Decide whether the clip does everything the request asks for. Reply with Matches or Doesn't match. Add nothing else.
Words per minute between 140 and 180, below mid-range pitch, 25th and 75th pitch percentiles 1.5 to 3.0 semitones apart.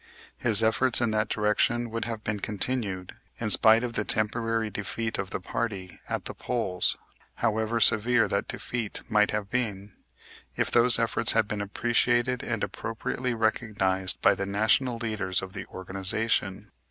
Matches